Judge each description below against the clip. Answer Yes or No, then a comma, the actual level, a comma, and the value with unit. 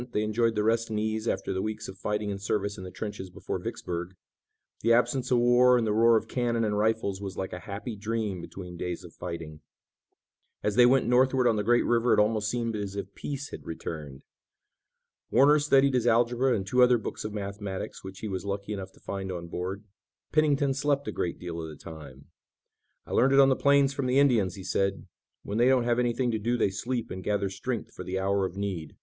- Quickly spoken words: Yes, fast, 225 wpm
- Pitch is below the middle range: Yes, low, 105 Hz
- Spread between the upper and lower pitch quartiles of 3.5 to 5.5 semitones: Yes, average, 4.2 semitones